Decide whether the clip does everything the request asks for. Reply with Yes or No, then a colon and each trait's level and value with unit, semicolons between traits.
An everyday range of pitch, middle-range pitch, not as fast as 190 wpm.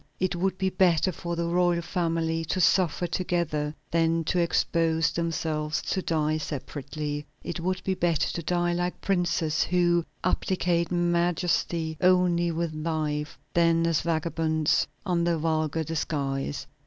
No: narrow, 1.9 semitones; medium, 170 Hz; average, 140 wpm